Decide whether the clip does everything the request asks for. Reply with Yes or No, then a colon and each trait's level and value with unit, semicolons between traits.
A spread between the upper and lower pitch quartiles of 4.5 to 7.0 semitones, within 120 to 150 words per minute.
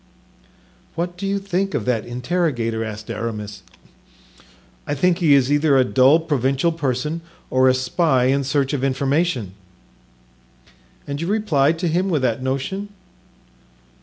Yes: average, 4.8 semitones; average, 140 wpm